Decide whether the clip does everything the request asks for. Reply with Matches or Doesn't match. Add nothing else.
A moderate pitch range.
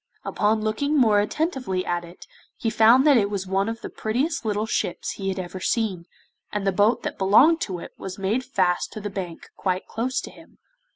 Matches